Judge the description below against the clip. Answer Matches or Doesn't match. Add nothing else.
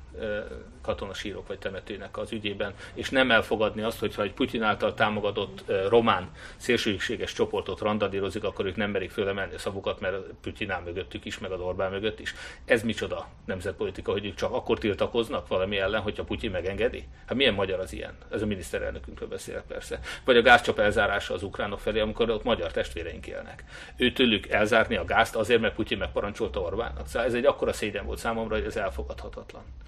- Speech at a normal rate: Doesn't match